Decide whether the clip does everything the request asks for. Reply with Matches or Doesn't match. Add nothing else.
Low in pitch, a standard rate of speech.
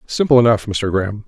Matches